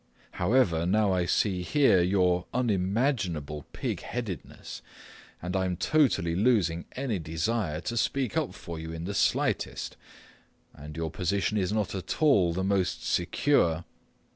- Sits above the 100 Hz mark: No, very low, 95 Hz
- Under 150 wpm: Yes, average, 140 wpm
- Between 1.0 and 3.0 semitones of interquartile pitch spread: No, average, 4.4 semitones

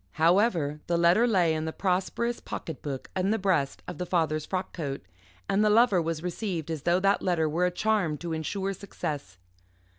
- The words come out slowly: No, average, 190 wpm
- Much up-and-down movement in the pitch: No, average, 3.7 semitones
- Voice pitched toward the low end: No, medium, 175 Hz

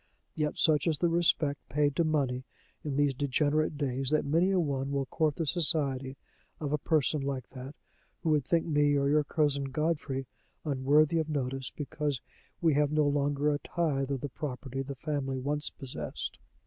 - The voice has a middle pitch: Yes, medium, 145 Hz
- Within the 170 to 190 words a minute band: Yes, average, 180 wpm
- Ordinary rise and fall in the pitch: No, narrow, 2.1 semitones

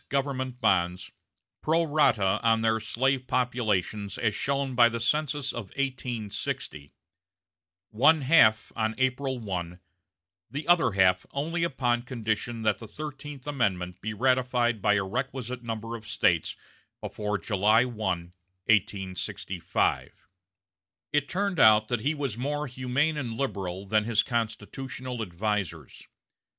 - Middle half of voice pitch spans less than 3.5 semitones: No, average, 4.4 semitones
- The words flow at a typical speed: No, slow, 125 wpm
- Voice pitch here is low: Yes, low, 115 Hz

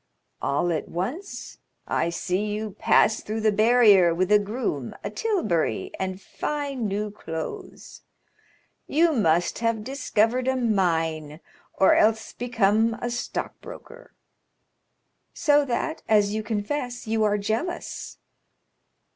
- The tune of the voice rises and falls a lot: No, average, 4.3 semitones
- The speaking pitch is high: Yes, high, 215 Hz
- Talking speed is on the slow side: Yes, slow, 120 wpm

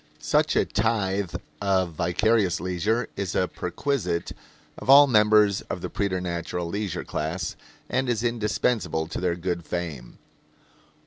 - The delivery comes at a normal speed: No, slow, 130 wpm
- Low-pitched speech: Yes, very low, 95 Hz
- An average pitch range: Yes, average, 4.0 semitones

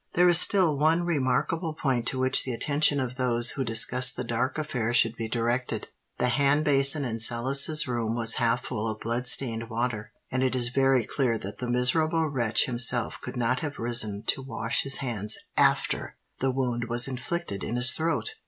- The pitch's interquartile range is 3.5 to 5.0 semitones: No, average, 2.9 semitones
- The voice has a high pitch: No, low, 125 Hz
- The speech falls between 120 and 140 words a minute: No, average, 190 wpm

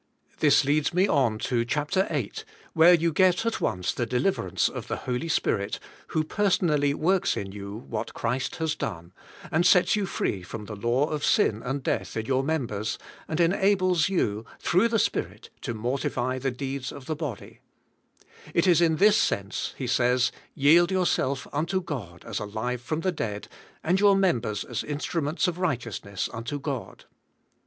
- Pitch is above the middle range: No, medium, 140 Hz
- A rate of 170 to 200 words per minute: Yes, average, 175 wpm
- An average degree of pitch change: No, wide, 6.9 semitones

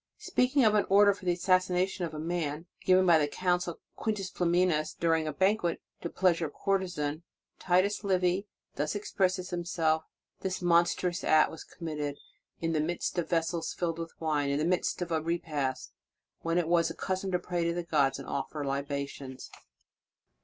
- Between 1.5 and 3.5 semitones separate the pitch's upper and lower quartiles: Yes, average, 2.9 semitones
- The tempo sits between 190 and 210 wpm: No, average, 180 wpm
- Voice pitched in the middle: Yes, medium, 170 Hz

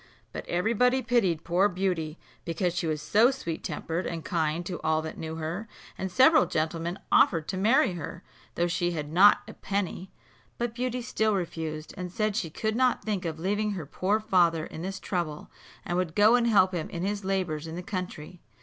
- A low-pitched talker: No, medium, 180 Hz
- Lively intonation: No, average, 4.2 semitones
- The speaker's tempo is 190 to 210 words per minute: Yes, average, 200 wpm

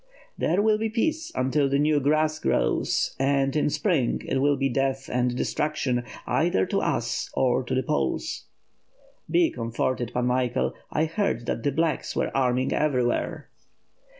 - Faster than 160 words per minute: No, average, 155 wpm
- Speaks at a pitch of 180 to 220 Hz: No, low, 135 Hz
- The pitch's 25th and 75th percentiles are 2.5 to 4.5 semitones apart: Yes, average, 3.6 semitones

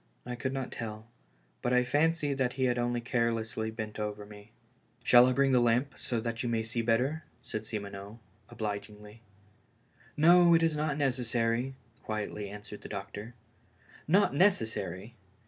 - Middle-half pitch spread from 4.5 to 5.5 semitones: No, average, 3.7 semitones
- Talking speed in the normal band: Yes, average, 155 wpm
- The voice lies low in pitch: Yes, low, 120 Hz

